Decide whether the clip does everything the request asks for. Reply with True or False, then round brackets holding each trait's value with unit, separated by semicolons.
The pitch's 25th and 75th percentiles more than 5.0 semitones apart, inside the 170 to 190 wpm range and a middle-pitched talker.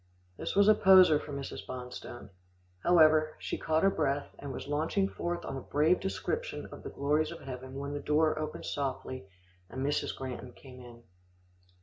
False (3.6 semitones; 180 wpm; 145 Hz)